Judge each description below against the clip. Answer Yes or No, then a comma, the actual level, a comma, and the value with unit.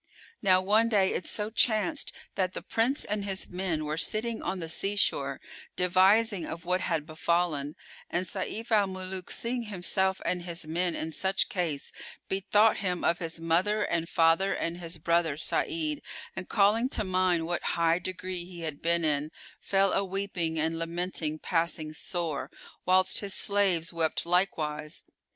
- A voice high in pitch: No, medium, 180 Hz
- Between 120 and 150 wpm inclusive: No, average, 165 wpm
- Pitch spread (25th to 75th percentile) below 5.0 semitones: Yes, average, 3.1 semitones